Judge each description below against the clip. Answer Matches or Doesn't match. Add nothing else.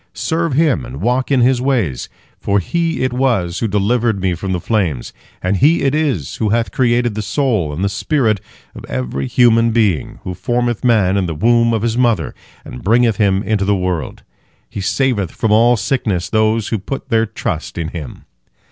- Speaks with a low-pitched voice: Matches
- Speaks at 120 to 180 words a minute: Doesn't match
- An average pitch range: Matches